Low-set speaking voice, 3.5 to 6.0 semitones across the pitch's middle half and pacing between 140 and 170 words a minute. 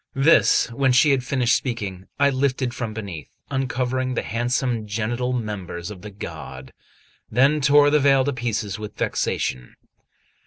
Yes: low, 120 Hz; average, 3.9 semitones; average, 150 wpm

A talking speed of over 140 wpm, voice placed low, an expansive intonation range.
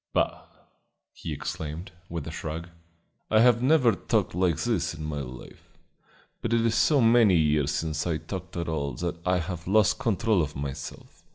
Yes: average, 175 wpm; very low, 85 Hz; wide, 6.0 semitones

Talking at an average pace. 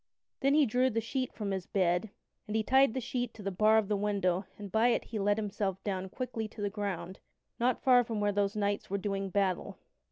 No: fast, 230 wpm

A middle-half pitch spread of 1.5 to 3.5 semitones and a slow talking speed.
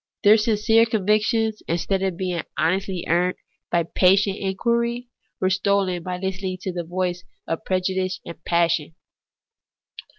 Yes: narrow, 2.6 semitones; slow, 130 wpm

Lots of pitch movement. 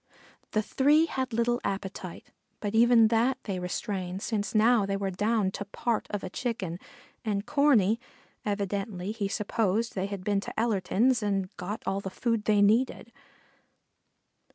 No: average, 2.8 semitones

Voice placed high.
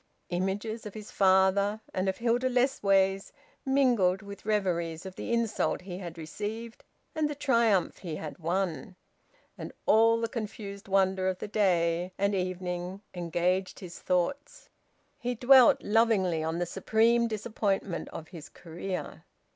Yes: high, 195 Hz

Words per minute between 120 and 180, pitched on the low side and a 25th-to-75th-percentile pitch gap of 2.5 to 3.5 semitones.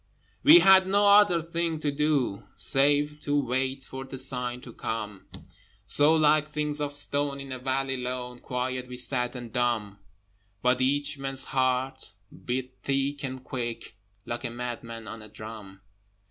Yes: average, 160 wpm; low, 130 Hz; average, 2.8 semitones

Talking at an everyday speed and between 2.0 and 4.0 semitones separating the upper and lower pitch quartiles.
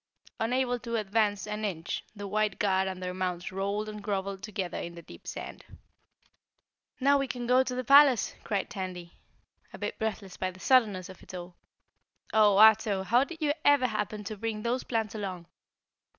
Yes: average, 185 wpm; average, 3.6 semitones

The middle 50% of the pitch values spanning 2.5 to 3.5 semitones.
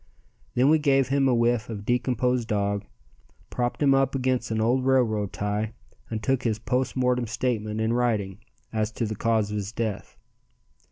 Yes: average, 3.0 semitones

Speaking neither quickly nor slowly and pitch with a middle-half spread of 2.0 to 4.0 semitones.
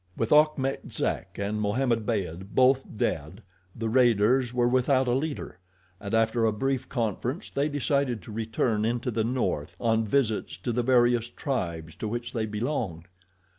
Yes: average, 160 wpm; average, 3.4 semitones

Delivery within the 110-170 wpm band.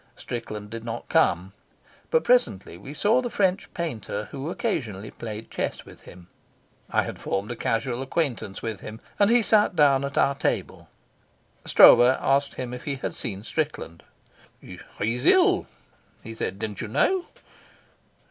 Yes: average, 155 wpm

